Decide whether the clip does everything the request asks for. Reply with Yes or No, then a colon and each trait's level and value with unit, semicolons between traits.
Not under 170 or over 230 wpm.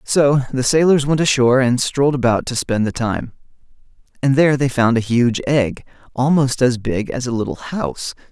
Yes: average, 190 wpm